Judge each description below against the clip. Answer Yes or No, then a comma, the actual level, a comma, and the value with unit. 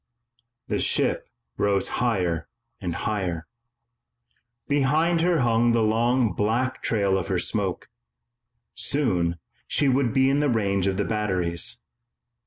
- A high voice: No, low, 110 Hz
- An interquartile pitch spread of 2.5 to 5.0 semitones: No, wide, 5.5 semitones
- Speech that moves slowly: Yes, slow, 125 wpm